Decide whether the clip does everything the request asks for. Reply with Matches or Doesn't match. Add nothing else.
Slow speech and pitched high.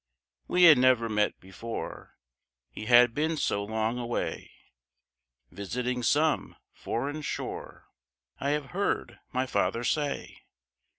Doesn't match